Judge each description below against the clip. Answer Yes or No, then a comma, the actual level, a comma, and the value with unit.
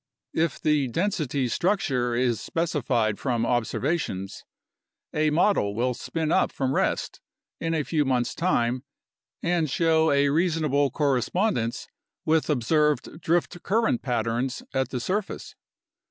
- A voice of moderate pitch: Yes, medium, 145 Hz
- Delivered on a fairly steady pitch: No, average, 5.0 semitones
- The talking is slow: Yes, slow, 125 wpm